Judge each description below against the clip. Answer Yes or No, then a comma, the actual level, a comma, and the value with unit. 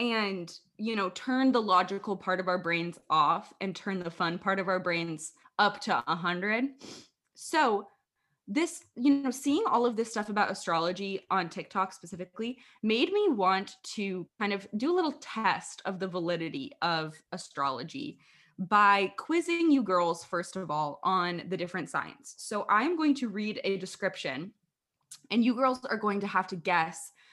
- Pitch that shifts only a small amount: No, average, 5.0 semitones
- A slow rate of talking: No, average, 175 wpm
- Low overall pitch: No, high, 195 Hz